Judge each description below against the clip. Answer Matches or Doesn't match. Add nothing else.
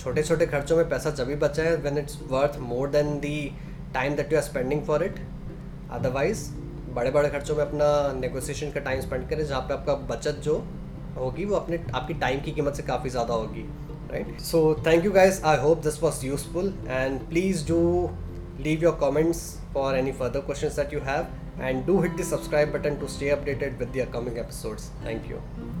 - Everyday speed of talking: Doesn't match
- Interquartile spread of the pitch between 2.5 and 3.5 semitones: Matches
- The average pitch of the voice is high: Doesn't match